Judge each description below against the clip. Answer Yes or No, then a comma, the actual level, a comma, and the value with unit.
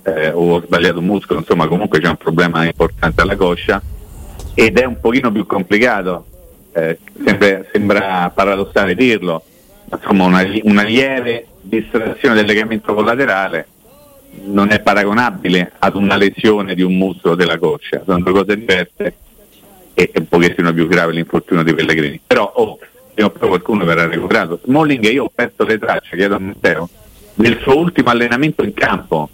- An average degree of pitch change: Yes, average, 3.4 semitones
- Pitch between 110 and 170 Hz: No, very low, 95 Hz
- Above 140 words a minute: Yes, average, 160 wpm